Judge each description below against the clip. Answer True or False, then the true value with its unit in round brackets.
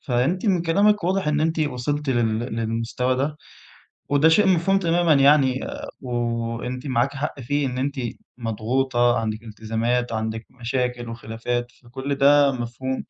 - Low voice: True (130 Hz)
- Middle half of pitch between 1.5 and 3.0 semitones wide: False (3.7 semitones)